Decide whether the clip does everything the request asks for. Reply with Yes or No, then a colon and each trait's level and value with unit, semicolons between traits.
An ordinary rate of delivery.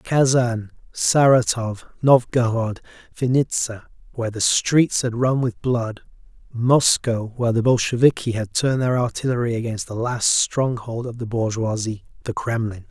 No: slow, 125 wpm